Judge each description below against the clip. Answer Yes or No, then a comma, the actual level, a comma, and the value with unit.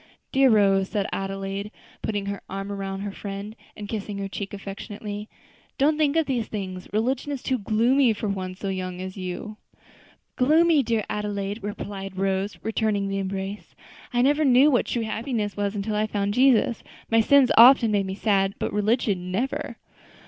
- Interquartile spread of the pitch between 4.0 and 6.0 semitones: No, average, 3.2 semitones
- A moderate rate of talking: Yes, average, 170 wpm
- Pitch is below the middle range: No, high, 205 Hz